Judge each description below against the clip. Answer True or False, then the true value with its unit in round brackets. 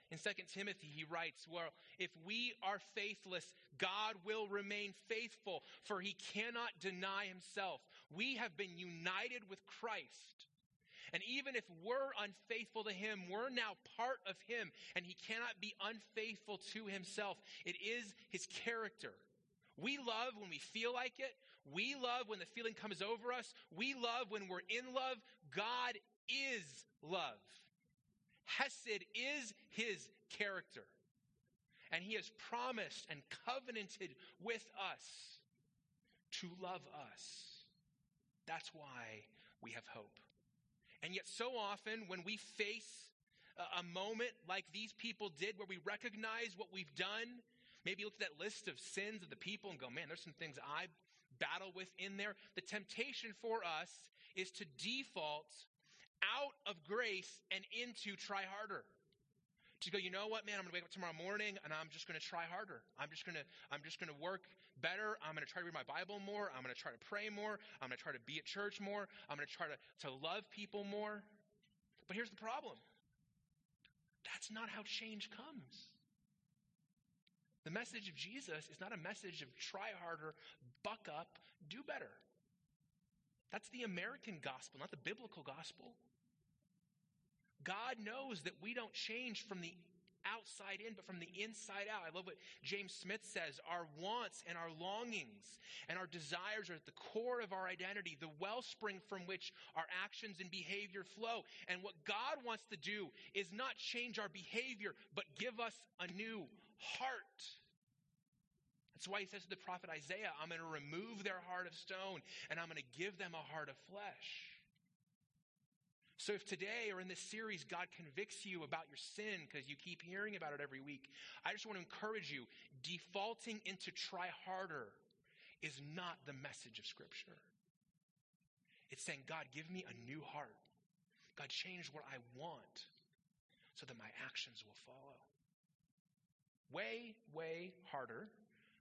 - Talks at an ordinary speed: True (165 wpm)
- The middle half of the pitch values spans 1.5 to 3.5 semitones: False (4.0 semitones)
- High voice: True (195 Hz)